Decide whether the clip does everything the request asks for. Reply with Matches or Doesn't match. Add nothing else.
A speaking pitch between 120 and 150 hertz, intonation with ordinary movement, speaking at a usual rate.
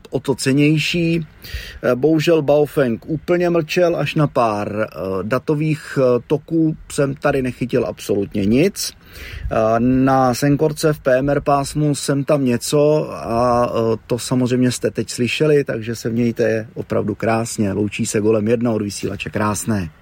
Matches